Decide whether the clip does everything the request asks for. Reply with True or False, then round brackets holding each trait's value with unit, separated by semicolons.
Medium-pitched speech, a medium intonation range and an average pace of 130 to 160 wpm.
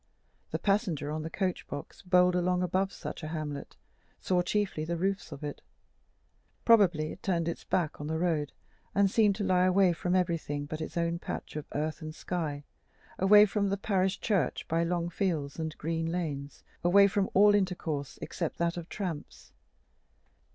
False (175 Hz; 3.4 semitones; 175 wpm)